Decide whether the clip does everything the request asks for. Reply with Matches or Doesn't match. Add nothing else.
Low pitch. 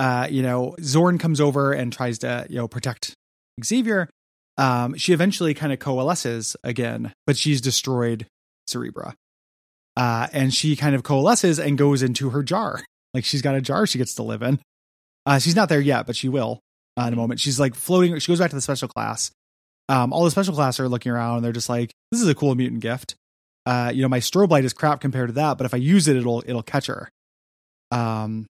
Matches